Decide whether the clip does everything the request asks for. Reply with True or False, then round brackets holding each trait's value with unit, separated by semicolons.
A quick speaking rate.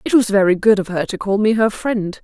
True (295 wpm)